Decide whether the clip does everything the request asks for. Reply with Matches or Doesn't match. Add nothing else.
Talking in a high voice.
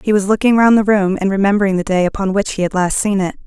Matches